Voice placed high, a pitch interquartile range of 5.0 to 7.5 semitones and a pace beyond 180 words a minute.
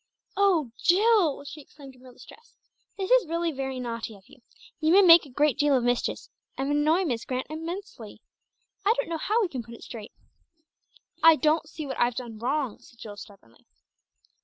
Yes: very high, 290 Hz; wide, 5.6 semitones; average, 190 wpm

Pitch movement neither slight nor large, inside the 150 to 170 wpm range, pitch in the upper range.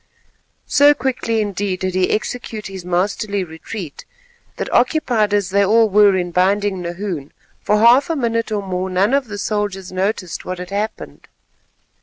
Yes: average, 3.1 semitones; average, 160 wpm; high, 205 Hz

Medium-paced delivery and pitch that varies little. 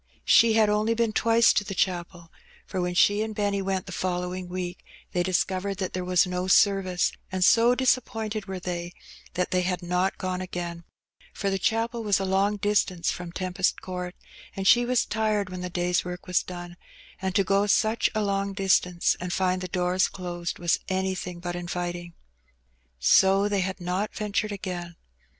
Yes: average, 185 wpm; narrow, 2.2 semitones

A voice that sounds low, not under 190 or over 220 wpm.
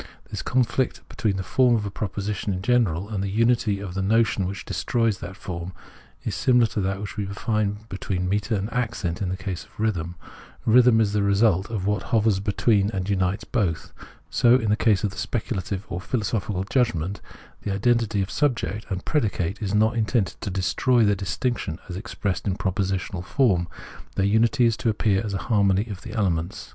Yes: low, 100 Hz; average, 195 wpm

